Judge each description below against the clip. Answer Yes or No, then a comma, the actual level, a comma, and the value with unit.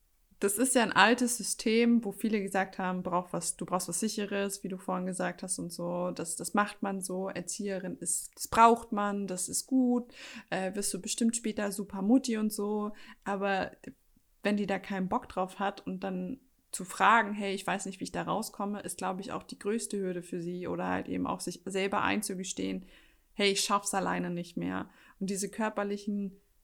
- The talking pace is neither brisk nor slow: No, fast, 200 wpm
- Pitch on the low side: No, high, 200 Hz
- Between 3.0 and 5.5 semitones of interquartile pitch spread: No, narrow, 2.4 semitones